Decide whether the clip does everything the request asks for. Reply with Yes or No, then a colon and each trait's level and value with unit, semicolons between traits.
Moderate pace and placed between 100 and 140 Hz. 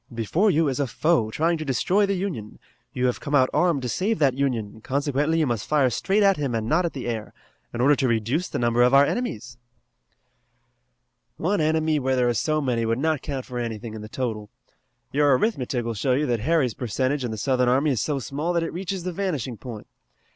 No: fast, 225 wpm; low, 135 Hz